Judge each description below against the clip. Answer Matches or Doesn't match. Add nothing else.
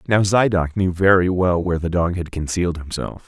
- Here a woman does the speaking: Doesn't match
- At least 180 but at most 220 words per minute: Matches